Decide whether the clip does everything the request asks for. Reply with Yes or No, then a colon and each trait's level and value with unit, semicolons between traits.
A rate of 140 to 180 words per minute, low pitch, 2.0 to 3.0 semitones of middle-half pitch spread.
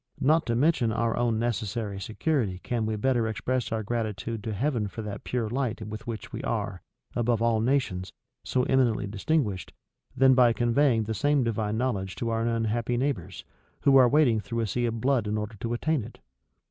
No: average, 190 wpm; low, 115 Hz; average, 2.7 semitones